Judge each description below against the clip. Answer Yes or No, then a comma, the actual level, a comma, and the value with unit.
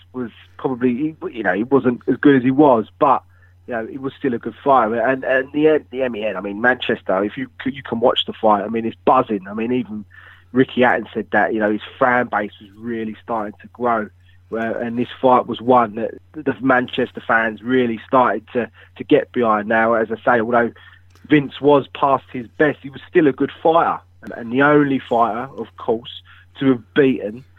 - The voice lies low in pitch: Yes, low, 115 Hz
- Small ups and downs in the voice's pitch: No, average, 3.7 semitones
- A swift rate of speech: Yes, fast, 210 wpm